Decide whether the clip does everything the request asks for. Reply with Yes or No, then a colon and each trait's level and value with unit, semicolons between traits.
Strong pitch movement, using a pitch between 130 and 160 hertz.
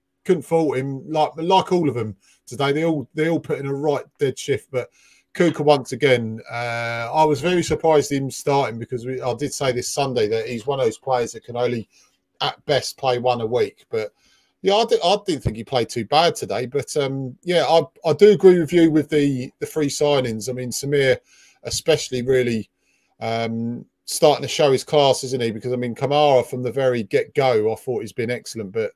No: average, 4.7 semitones; medium, 140 Hz